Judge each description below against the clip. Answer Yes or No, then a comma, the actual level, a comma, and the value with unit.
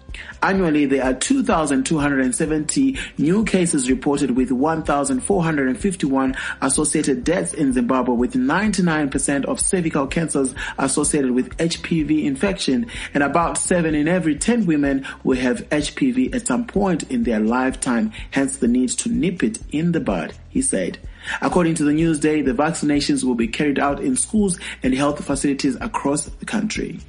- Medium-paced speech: Yes, average, 150 wpm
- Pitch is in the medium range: Yes, medium, 155 Hz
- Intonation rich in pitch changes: Yes, wide, 6.3 semitones